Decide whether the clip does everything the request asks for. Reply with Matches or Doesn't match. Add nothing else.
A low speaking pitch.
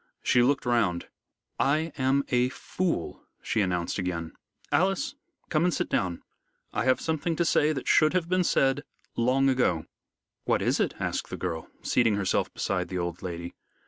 Matches